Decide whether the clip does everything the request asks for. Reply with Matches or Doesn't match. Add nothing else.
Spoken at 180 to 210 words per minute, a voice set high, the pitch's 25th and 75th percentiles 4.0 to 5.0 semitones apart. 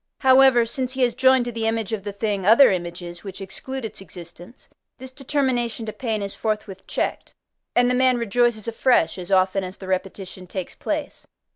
Matches